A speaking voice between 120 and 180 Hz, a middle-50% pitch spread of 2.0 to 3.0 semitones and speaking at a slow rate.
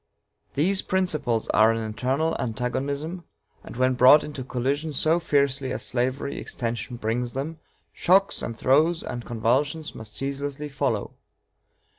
No: low, 135 Hz; average, 3.8 semitones; slow, 130 wpm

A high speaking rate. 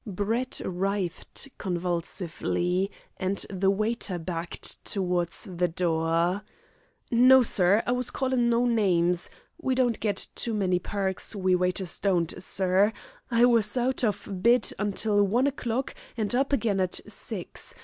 No: slow, 135 wpm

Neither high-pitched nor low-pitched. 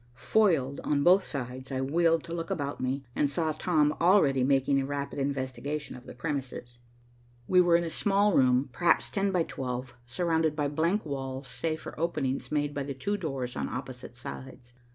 Yes: medium, 145 Hz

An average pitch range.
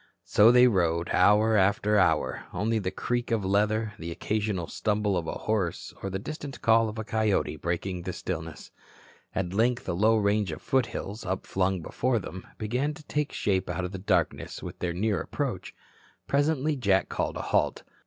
Yes: average, 3.5 semitones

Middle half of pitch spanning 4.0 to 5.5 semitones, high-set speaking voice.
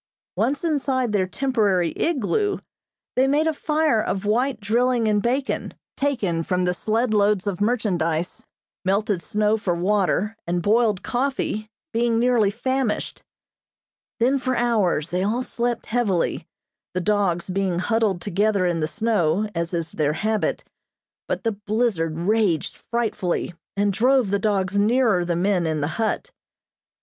Yes: average, 4.7 semitones; high, 210 Hz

